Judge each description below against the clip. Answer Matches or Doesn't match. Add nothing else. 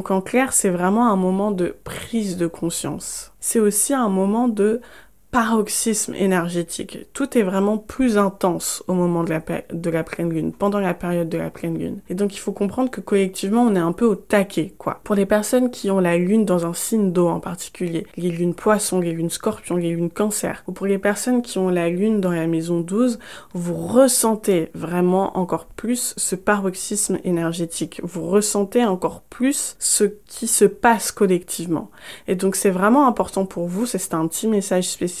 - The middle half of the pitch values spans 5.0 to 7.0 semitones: Doesn't match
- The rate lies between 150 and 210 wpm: Matches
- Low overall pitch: Doesn't match